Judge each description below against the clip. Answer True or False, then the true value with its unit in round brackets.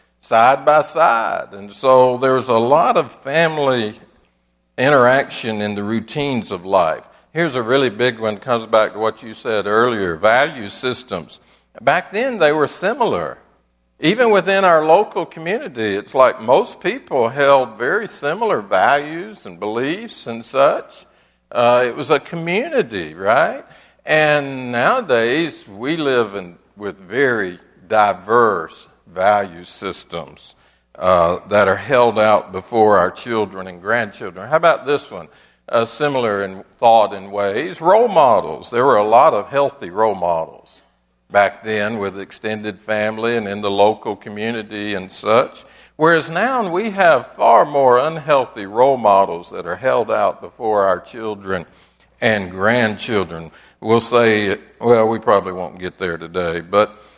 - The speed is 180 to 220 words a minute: False (145 wpm)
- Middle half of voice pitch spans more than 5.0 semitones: True (5.4 semitones)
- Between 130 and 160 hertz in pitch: False (115 Hz)